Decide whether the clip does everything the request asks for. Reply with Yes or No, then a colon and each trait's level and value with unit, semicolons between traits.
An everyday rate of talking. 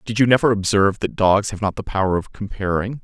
No: fast, 235 wpm